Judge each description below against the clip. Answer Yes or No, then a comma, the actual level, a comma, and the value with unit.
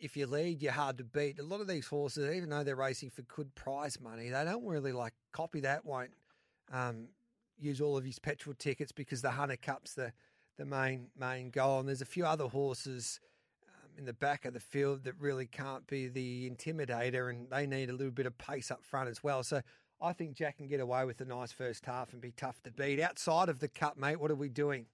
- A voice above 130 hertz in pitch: Yes, medium, 140 Hz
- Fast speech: Yes, fast, 240 wpm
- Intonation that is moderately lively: No, narrow, 2.3 semitones